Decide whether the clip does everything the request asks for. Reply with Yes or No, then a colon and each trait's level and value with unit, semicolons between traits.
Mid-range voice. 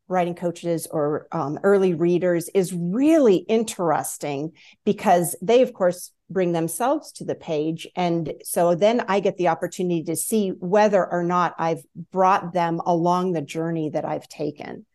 Yes: medium, 175 Hz